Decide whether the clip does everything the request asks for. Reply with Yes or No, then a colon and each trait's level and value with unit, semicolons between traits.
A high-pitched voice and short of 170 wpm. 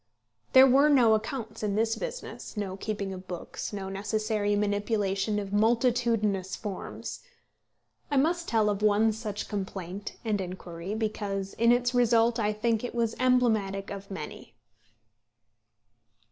Yes: high, 215 Hz; slow, 135 wpm